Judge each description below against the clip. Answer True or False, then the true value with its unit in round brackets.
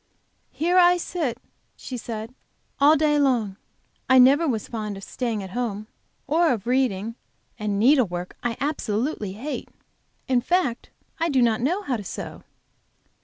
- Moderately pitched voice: False (245 Hz)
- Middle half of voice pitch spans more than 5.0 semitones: True (5.4 semitones)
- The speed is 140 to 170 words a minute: True (150 wpm)